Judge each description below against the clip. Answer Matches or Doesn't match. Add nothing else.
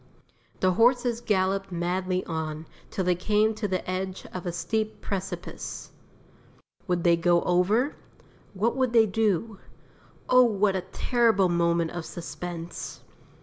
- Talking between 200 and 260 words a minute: Doesn't match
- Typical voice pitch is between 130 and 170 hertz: Doesn't match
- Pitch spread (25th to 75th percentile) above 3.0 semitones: Matches